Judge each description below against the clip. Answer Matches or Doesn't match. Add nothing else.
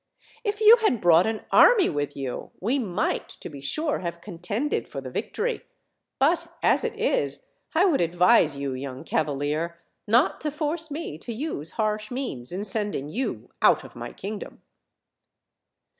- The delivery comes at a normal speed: Matches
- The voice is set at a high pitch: Matches